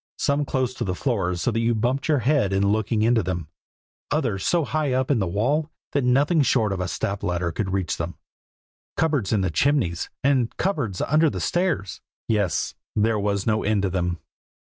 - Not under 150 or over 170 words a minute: No, average, 195 wpm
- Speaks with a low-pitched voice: Yes, low, 110 Hz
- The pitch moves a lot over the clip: Yes, wide, 6.3 semitones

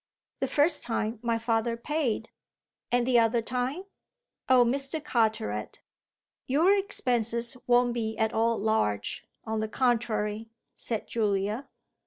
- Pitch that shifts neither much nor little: No, narrow, 2.3 semitones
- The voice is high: Yes, high, 235 Hz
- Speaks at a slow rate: Yes, slow, 125 wpm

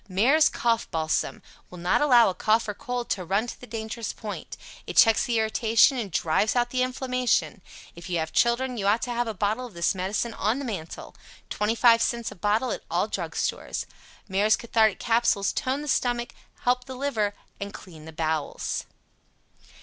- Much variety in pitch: No, average, 3.6 semitones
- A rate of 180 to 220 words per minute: Yes, average, 185 wpm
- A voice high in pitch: Yes, high, 225 Hz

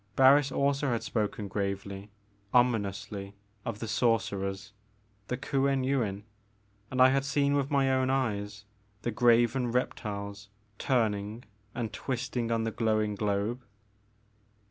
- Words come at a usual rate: No, slow, 120 wpm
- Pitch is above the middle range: No, low, 115 Hz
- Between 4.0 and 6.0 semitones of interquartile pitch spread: Yes, average, 4.3 semitones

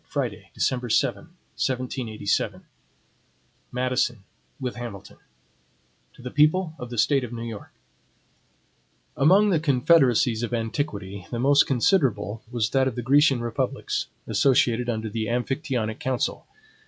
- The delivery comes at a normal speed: No, slow, 125 wpm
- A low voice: Yes, low, 125 Hz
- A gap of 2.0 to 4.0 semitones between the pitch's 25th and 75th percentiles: Yes, average, 3.1 semitones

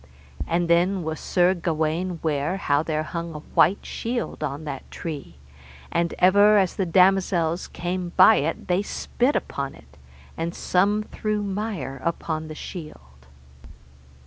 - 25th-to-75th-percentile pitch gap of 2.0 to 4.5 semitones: Yes, average, 3.5 semitones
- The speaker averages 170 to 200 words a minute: No, average, 145 wpm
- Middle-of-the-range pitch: Yes, medium, 170 Hz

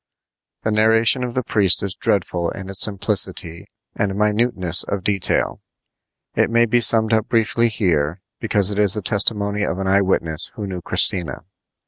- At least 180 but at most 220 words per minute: No, average, 165 wpm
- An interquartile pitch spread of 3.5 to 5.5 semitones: No, average, 2.9 semitones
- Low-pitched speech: Yes, low, 100 Hz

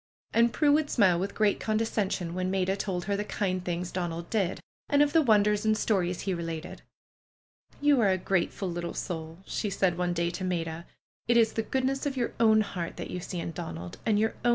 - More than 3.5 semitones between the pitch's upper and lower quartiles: Yes, average, 4.0 semitones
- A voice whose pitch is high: Yes, high, 195 Hz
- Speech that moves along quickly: Yes, fast, 215 wpm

